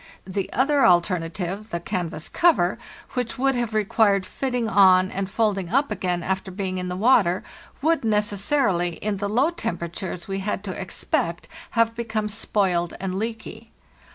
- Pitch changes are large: No, average, 3.8 semitones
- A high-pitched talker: Yes, high, 200 Hz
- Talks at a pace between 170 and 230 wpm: No, average, 150 wpm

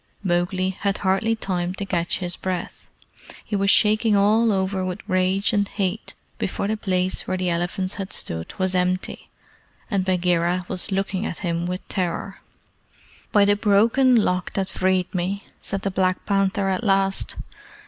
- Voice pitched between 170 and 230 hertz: Yes, high, 190 Hz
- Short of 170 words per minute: Yes, average, 160 wpm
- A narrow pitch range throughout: Yes, narrow, 1.7 semitones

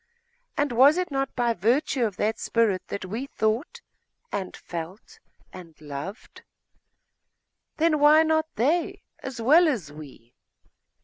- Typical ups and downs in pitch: No, wide, 8.2 semitones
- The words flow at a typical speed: No, slow, 130 wpm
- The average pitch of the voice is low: No, high, 235 Hz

